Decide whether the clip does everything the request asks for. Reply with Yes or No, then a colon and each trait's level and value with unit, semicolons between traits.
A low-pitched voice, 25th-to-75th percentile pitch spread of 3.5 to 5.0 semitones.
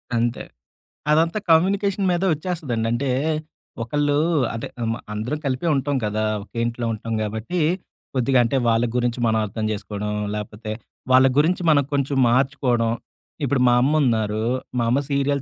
Yes: low, 125 Hz; average, 4.2 semitones